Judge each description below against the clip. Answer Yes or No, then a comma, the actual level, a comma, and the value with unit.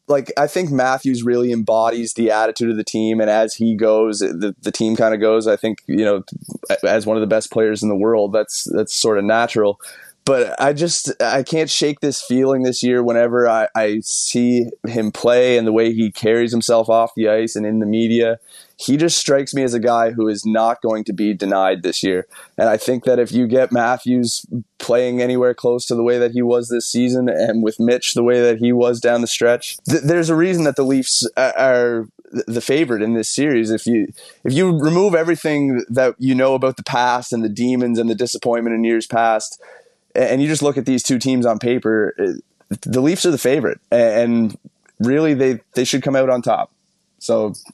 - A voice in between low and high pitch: No, low, 120 Hz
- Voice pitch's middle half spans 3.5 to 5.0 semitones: No, average, 2.7 semitones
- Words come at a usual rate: No, fast, 215 wpm